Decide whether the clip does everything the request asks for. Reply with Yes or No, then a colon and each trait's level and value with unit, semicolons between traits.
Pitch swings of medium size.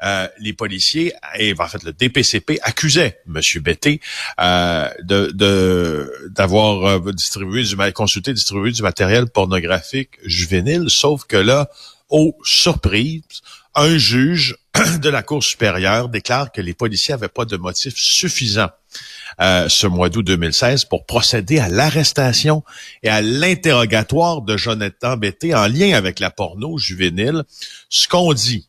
No: wide, 6.4 semitones